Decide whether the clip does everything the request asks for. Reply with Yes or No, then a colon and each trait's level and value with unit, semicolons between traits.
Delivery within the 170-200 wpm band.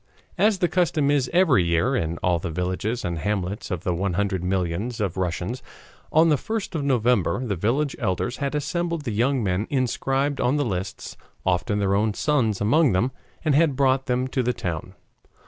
Yes: average, 190 wpm